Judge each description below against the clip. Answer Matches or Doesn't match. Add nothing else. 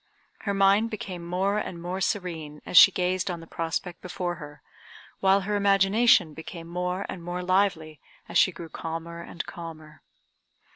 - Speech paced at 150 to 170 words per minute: Matches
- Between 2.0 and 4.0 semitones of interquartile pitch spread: Matches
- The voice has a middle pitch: Matches